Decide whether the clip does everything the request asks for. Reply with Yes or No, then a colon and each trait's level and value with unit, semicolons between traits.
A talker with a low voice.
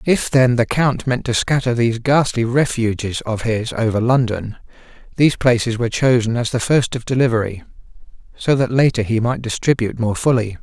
Yes: low, 120 Hz